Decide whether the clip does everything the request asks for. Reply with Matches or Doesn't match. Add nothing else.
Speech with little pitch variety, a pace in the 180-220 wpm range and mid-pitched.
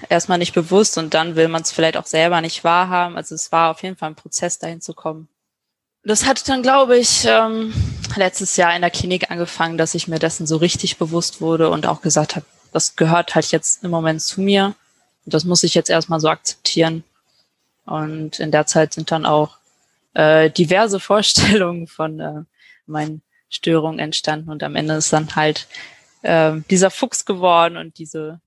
Matches